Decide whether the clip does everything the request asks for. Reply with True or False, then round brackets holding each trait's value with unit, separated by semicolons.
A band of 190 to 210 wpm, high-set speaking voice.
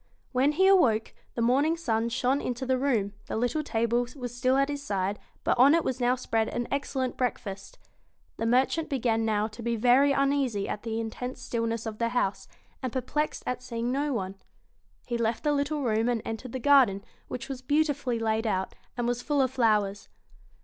True (195 wpm; 245 Hz)